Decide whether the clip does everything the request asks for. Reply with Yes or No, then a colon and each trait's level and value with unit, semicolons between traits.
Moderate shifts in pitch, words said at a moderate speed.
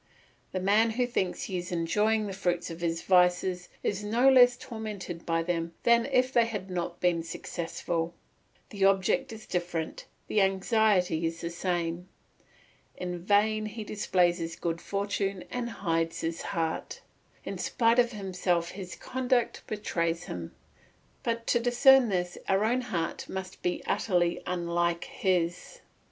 Yes: average, 4.2 semitones; average, 150 wpm